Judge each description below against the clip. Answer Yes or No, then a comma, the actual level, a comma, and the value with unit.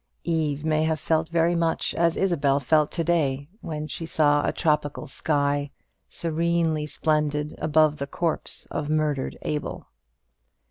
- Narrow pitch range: Yes, narrow, 1.8 semitones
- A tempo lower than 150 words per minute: Yes, average, 140 wpm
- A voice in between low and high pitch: Yes, medium, 155 Hz